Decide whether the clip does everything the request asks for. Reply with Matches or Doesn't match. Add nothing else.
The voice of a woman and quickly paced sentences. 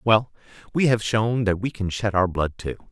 Doesn't match